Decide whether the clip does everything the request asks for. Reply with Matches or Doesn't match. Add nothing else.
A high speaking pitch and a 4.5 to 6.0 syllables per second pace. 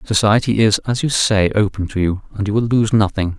Doesn't match